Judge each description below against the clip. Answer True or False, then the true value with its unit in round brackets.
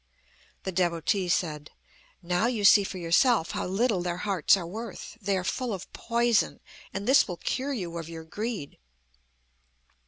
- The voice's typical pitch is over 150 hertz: True (190 Hz)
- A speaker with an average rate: True (160 wpm)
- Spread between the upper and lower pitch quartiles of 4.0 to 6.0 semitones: True (4.8 semitones)